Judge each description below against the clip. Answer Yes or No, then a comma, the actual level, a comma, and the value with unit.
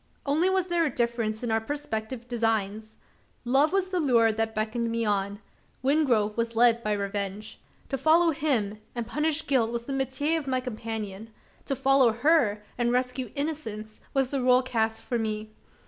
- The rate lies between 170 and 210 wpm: Yes, average, 175 wpm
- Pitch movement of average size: Yes, average, 3.9 semitones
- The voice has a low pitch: No, high, 235 Hz